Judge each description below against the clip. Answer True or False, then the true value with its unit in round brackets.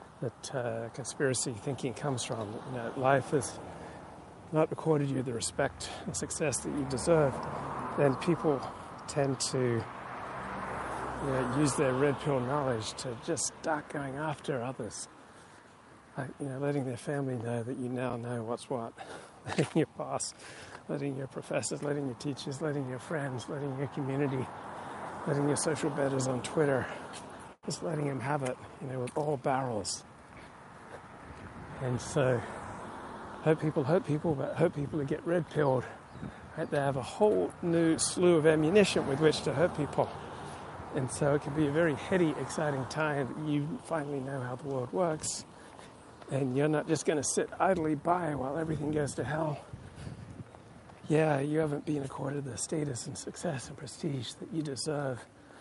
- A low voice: False (145 Hz)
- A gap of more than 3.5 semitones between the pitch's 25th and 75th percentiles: False (3.0 semitones)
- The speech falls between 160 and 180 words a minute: True (165 wpm)